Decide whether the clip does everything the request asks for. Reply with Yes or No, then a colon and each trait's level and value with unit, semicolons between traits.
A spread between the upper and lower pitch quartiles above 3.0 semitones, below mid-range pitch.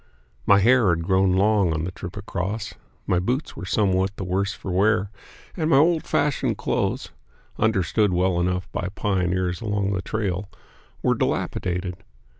No: average, 2.7 semitones; very low, 95 Hz